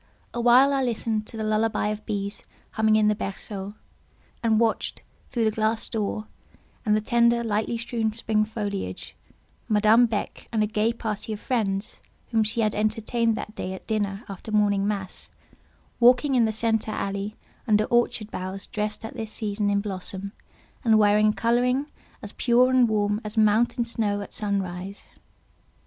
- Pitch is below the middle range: No, high, 215 Hz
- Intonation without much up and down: Yes, narrow, 2.0 semitones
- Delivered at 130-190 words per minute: Yes, average, 165 wpm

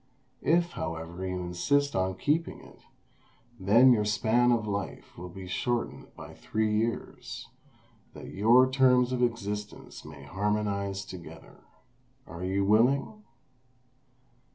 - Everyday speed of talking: No, slow, 120 wpm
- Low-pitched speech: Yes, low, 105 Hz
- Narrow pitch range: No, average, 4.7 semitones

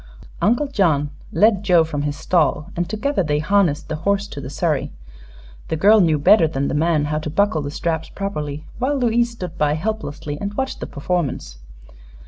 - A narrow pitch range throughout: No, wide, 5.5 semitones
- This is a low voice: No, medium, 165 Hz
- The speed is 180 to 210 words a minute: Yes, average, 185 wpm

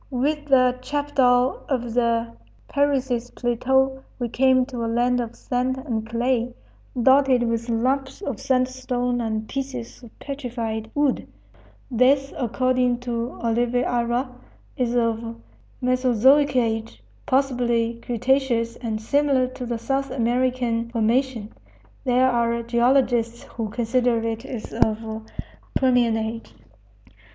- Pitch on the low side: No, high, 245 Hz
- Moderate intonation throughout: No, narrow, 2.0 semitones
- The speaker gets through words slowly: Yes, slow, 115 wpm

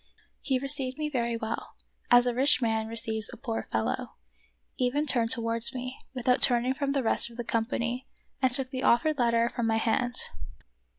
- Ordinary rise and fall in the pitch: No, narrow, 2.2 semitones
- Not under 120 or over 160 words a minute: No, average, 190 wpm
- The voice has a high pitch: Yes, high, 245 Hz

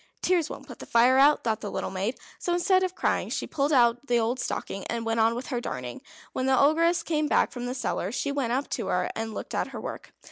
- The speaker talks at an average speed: No, fast, 255 wpm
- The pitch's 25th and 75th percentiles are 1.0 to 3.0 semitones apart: No, average, 4.1 semitones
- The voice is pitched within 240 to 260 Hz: Yes, very high, 250 Hz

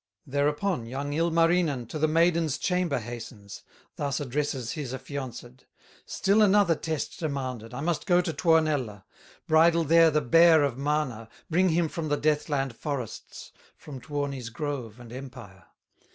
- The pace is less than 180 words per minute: Yes, average, 145 wpm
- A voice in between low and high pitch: Yes, medium, 145 Hz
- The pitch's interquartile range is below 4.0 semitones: No, average, 4.4 semitones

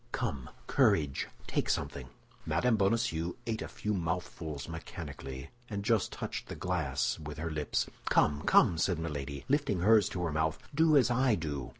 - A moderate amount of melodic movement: No, wide, 6.1 semitones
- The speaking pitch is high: No, very low, 85 Hz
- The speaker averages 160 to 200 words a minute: Yes, average, 165 wpm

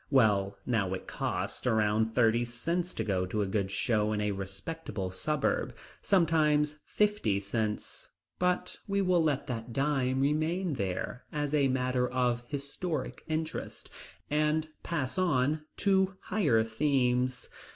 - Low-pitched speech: Yes, low, 130 Hz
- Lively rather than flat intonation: Yes, wide, 6.0 semitones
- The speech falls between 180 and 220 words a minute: No, slow, 135 wpm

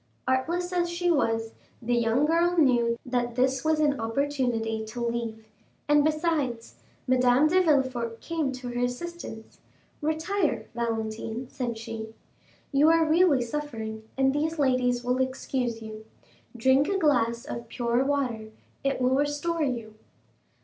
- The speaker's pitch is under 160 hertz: No, very high, 255 Hz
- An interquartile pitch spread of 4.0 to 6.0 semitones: Yes, average, 4.3 semitones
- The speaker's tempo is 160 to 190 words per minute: No, average, 140 wpm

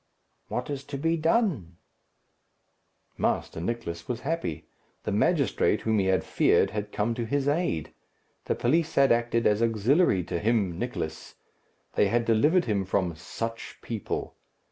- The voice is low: Yes, low, 115 Hz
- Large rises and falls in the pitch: Yes, wide, 6.1 semitones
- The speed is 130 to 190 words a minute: Yes, average, 145 wpm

